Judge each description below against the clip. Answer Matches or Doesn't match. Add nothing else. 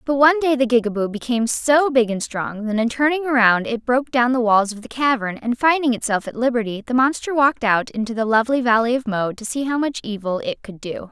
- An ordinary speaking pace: Doesn't match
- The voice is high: Matches